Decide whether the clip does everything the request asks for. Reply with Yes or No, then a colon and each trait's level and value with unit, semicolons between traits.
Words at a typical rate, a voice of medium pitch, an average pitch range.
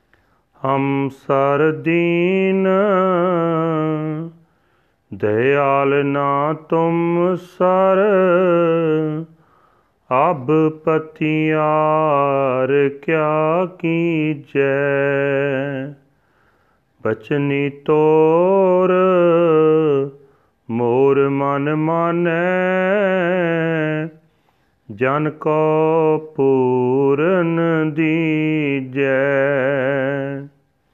No: slow, 35 wpm; medium, 155 Hz; average, 3.1 semitones